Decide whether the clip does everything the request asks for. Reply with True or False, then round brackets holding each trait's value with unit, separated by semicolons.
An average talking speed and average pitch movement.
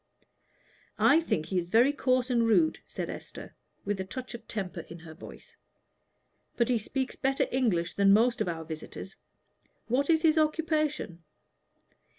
False (160 wpm; 6.8 semitones)